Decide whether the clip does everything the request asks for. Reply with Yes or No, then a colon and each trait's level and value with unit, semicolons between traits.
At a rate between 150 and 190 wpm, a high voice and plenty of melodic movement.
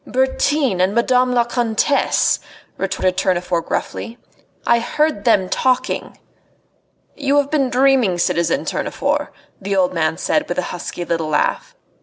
No: slow, 135 wpm; high, 235 Hz; wide, 6.3 semitones